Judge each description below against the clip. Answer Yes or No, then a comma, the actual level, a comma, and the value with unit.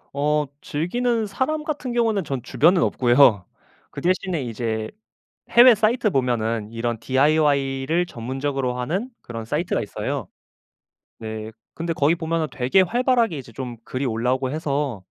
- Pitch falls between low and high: Yes, medium, 145 Hz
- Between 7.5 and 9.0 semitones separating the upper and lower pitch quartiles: No, wide, 7.1 semitones